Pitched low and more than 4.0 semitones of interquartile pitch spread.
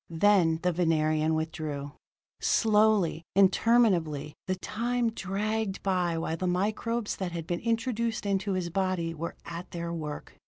No: medium, 185 Hz; average, 4.4 semitones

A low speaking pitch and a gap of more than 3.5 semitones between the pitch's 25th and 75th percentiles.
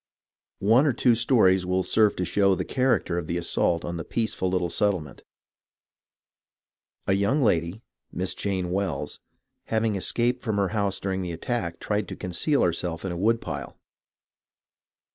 Yes: very low, 95 Hz; average, 4.0 semitones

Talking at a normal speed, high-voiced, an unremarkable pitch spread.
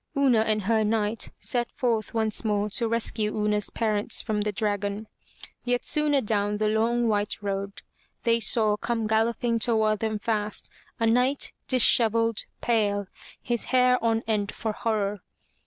No: average, 150 wpm; high, 220 Hz; narrow, 1.8 semitones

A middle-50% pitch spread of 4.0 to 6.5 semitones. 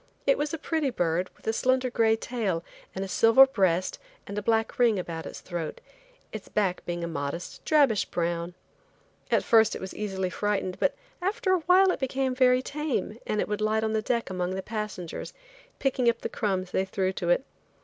Yes: wide, 5.5 semitones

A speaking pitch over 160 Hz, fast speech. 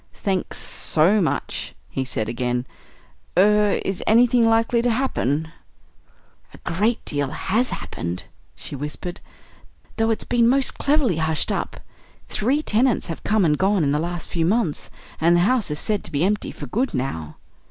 No: high, 190 Hz; average, 165 wpm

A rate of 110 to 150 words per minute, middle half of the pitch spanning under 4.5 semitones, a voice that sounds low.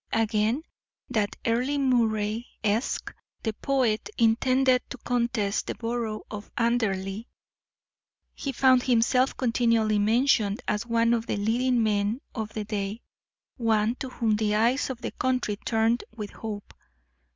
No: slow, 135 wpm; narrow, 2.6 semitones; high, 230 Hz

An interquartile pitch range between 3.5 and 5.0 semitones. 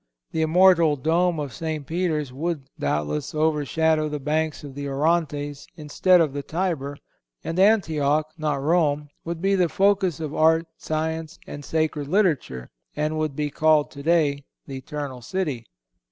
No: narrow, 2.4 semitones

